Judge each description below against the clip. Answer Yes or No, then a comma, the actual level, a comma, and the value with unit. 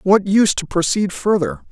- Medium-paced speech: Yes, average, 175 wpm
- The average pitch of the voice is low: No, high, 195 Hz